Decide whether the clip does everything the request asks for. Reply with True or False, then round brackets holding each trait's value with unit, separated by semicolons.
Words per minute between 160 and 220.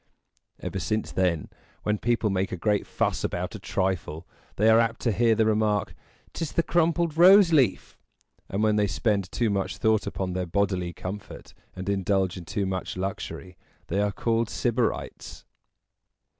True (165 wpm)